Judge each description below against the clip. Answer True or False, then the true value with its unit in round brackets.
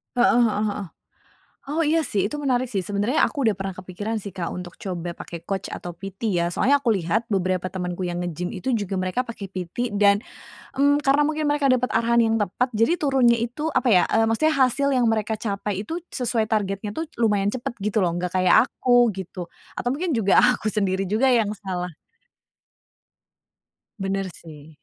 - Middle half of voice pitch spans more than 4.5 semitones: True (5.0 semitones)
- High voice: True (210 Hz)